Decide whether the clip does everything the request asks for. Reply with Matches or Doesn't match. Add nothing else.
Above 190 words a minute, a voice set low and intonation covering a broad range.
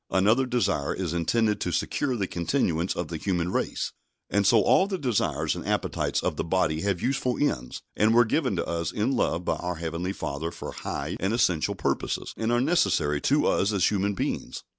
Matches